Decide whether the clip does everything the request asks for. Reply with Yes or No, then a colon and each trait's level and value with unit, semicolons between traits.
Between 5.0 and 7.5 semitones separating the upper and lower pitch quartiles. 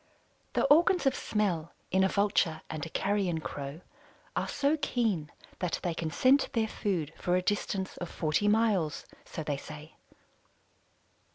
Yes: average, 5.3 semitones